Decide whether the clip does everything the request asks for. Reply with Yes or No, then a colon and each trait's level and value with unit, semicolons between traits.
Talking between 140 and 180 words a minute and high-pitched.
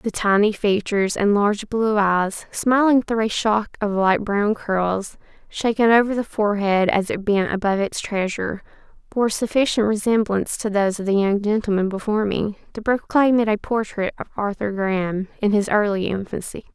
Yes: average, 170 wpm; high, 210 Hz